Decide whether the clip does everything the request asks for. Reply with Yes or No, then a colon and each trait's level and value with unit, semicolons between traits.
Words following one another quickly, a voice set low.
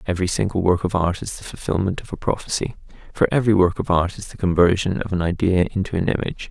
Yes: fast, 230 wpm; very low, 90 Hz